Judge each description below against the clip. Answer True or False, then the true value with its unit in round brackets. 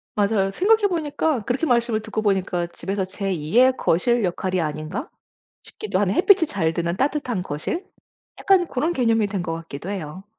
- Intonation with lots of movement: True (7.2 semitones)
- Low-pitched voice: False (205 Hz)